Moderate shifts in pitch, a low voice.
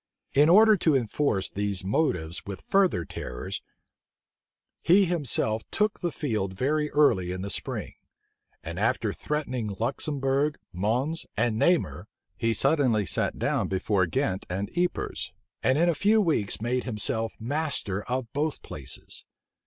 No: wide, 7.3 semitones; low, 120 Hz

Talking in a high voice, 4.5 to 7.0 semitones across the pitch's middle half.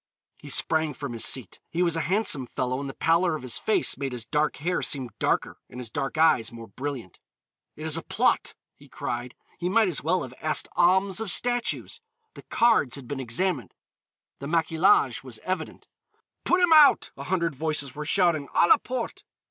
No: medium, 155 Hz; wide, 5.4 semitones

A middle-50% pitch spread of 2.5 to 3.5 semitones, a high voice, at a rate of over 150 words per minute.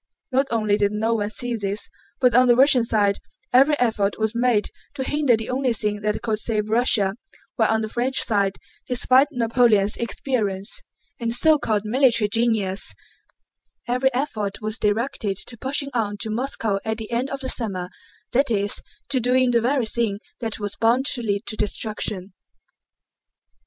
Yes: average, 3.2 semitones; high, 230 Hz; average, 170 wpm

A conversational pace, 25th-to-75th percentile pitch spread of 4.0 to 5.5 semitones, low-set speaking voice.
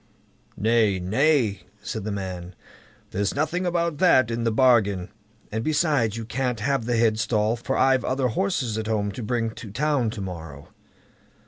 Yes: average, 160 wpm; average, 4.3 semitones; low, 115 Hz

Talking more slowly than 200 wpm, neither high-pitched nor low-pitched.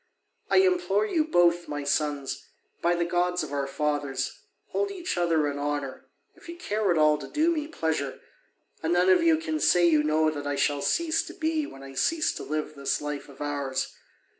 No: fast, 205 wpm; medium, 160 Hz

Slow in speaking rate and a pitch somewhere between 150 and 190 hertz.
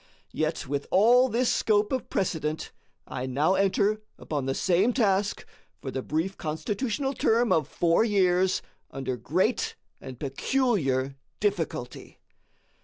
Yes: slow, 125 wpm; medium, 185 Hz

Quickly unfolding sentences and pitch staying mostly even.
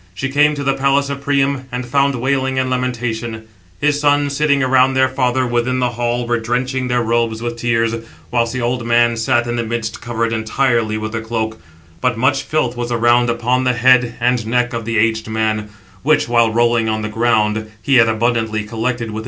Yes: fast, 220 wpm; narrow, 2.2 semitones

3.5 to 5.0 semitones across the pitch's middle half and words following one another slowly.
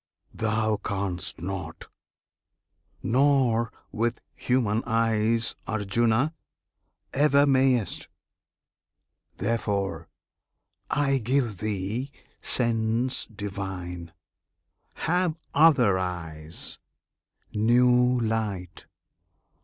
Yes: average, 4.1 semitones; slow, 65 wpm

